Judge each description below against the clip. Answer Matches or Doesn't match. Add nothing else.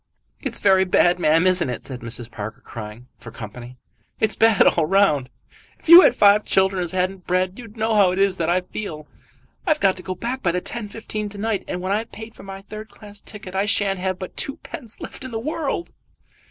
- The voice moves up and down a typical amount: Matches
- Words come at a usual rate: Doesn't match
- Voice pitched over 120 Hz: Matches